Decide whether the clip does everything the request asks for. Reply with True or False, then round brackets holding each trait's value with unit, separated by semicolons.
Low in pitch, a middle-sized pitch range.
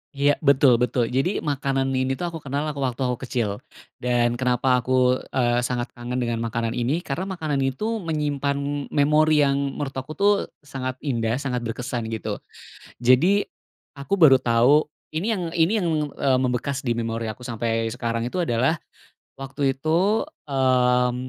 True (130 Hz; 3.0 semitones)